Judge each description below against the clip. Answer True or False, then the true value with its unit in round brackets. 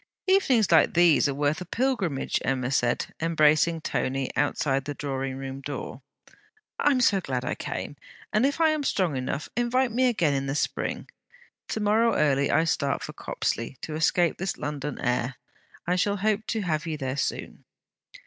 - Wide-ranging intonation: True (7.6 semitones)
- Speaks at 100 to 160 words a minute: False (175 wpm)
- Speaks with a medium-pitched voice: True (155 Hz)